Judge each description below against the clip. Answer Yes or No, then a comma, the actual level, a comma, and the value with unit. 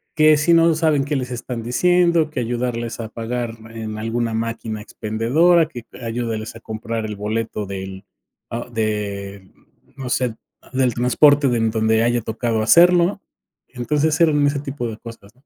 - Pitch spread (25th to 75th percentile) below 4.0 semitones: No, average, 4.5 semitones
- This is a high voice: No, low, 120 Hz